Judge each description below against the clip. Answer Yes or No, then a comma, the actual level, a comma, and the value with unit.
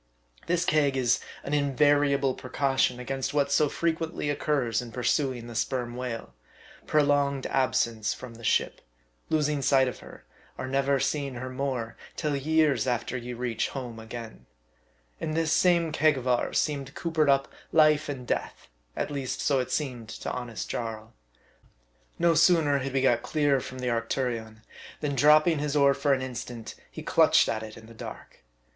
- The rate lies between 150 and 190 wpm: Yes, average, 170 wpm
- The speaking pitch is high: No, low, 135 Hz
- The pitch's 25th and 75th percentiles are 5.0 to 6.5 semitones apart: No, average, 3.2 semitones